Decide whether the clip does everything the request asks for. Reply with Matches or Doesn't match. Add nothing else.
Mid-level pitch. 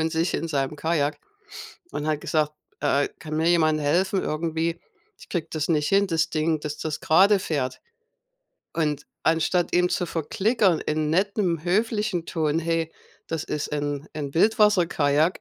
Matches